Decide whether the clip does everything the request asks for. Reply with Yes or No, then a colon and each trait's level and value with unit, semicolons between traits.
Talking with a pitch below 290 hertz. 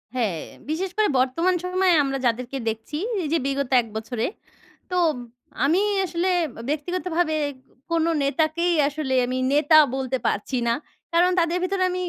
No: very high, 310 Hz